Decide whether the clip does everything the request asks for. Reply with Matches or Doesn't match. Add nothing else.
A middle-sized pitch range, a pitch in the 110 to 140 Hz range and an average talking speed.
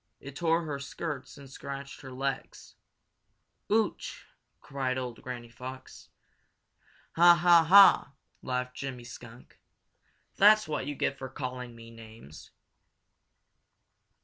Doesn't match